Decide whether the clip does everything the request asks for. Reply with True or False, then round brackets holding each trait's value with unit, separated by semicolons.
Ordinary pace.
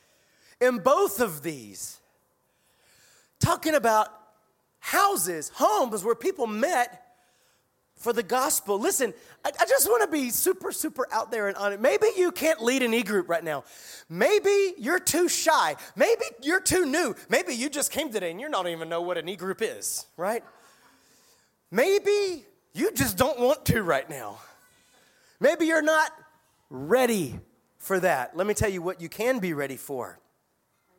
True (165 wpm)